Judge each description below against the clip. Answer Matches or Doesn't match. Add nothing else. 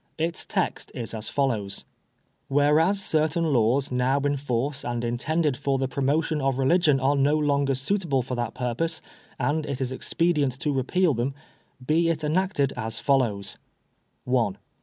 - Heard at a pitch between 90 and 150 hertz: Matches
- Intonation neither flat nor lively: Matches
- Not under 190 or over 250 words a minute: Doesn't match